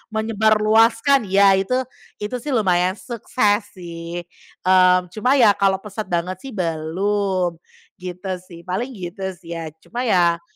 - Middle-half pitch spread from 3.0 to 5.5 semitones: Yes, average, 3.4 semitones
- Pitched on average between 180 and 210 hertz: Yes, high, 190 Hz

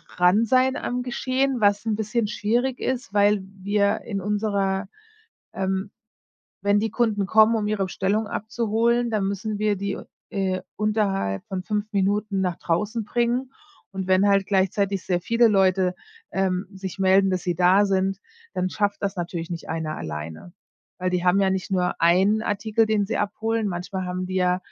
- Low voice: No, high, 200 Hz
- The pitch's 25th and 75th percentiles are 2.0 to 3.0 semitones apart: Yes, narrow, 2.4 semitones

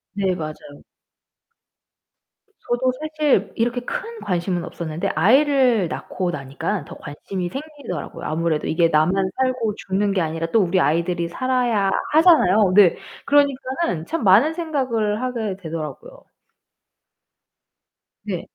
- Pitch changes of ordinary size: No, wide, 7.2 semitones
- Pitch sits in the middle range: No, high, 200 Hz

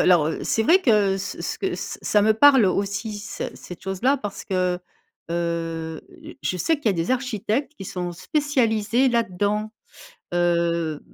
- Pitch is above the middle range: Yes, high, 200 Hz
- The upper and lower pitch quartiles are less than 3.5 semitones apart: No, average, 4.8 semitones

